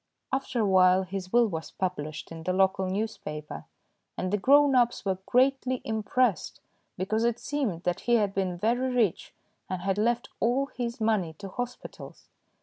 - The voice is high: Yes, high, 210 Hz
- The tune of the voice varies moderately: Yes, average, 4.6 semitones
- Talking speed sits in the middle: Yes, average, 165 wpm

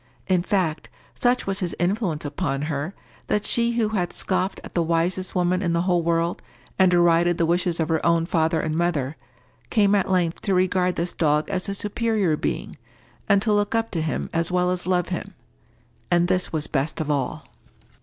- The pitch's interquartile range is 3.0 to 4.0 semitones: No, narrow, 2.5 semitones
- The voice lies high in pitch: No, medium, 175 Hz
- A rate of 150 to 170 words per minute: No, average, 195 wpm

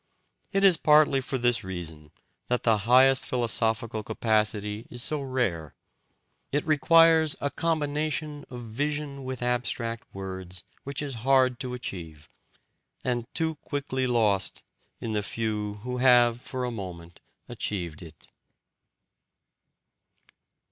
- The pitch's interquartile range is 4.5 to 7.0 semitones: Yes, average, 4.8 semitones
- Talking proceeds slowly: Yes, slow, 120 wpm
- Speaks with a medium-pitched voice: No, low, 125 Hz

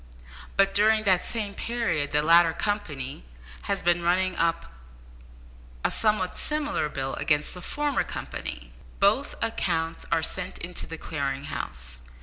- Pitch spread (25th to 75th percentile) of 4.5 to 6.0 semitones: Yes, wide, 5.5 semitones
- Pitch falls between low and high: Yes, medium, 175 Hz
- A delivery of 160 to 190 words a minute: No, average, 140 wpm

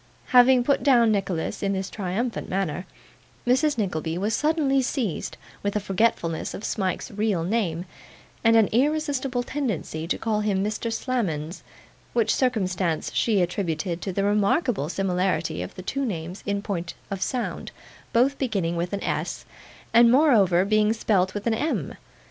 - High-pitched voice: Yes, high, 205 Hz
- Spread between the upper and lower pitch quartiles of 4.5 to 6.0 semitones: Yes, average, 4.9 semitones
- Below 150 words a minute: No, average, 155 wpm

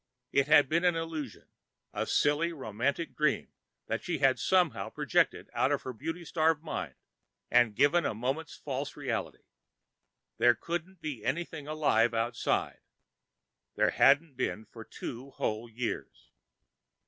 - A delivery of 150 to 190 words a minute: No, average, 140 wpm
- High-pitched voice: No, medium, 140 Hz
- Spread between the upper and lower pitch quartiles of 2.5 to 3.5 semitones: No, average, 5.2 semitones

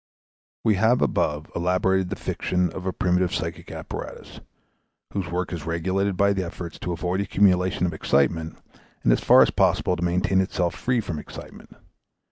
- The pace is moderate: Yes, average, 165 wpm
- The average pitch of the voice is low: Yes, very low, 90 Hz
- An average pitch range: No, narrow, 1.9 semitones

